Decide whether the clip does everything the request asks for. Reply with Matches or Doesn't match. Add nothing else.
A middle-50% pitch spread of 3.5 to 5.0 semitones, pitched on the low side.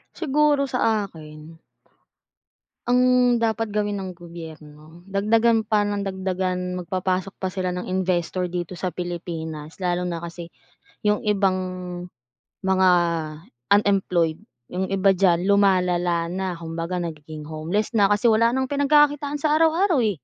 Doesn't match